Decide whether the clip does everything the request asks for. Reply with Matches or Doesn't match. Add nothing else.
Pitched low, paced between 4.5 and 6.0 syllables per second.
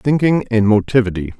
Matches